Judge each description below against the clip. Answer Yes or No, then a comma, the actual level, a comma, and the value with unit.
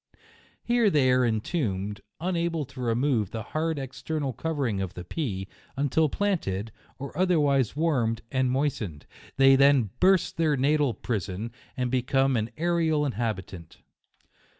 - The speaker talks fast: No, average, 145 wpm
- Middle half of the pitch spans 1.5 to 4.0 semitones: No, wide, 5.5 semitones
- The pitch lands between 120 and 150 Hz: Yes, low, 135 Hz